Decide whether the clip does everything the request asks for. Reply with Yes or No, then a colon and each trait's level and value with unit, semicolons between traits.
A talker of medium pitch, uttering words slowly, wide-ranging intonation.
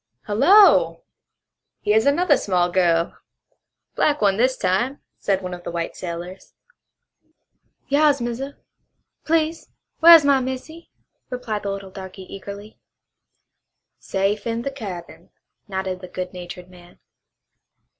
No: high, 205 Hz; slow, 120 wpm; wide, 6.8 semitones